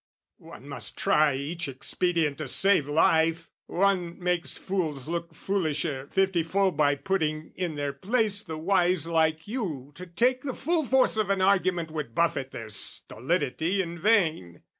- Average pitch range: Yes, average, 4.0 semitones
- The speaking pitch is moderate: Yes, medium, 170 Hz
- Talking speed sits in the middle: Yes, average, 155 wpm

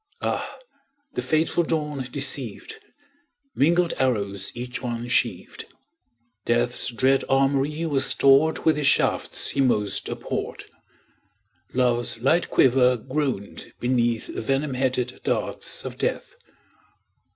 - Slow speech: Yes, slow, 105 wpm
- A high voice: No, low, 130 Hz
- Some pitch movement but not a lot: Yes, average, 3.5 semitones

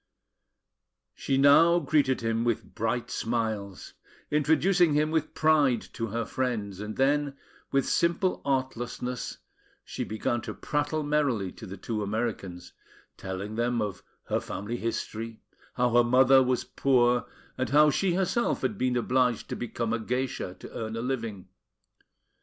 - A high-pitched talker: No, low, 125 Hz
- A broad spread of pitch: No, average, 4.0 semitones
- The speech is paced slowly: No, average, 145 wpm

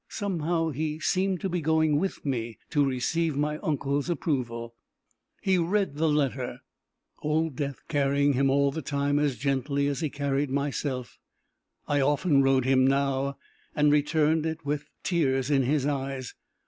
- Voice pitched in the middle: Yes, medium, 145 Hz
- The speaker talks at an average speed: Yes, average, 160 wpm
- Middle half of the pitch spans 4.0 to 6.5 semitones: No, narrow, 2.5 semitones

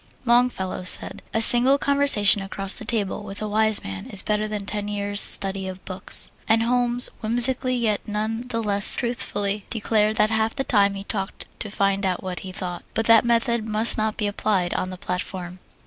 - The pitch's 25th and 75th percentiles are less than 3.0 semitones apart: Yes, narrow, 2.6 semitones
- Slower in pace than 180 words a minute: No, average, 195 wpm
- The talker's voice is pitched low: No, high, 210 Hz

